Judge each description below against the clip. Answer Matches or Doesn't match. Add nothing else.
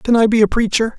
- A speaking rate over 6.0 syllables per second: Matches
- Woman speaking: Doesn't match